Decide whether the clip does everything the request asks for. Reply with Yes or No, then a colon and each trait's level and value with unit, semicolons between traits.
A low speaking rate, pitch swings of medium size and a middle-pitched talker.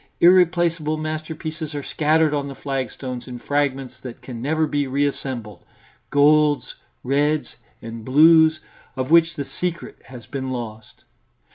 Yes: slow, 130 wpm; average, 3.3 semitones; medium, 145 Hz